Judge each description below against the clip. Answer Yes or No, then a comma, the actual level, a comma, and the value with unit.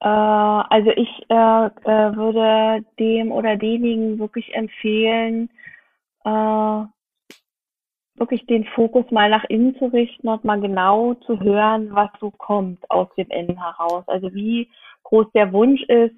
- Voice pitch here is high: Yes, high, 220 Hz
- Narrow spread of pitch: Yes, narrow, 1.6 semitones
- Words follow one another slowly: No, average, 135 wpm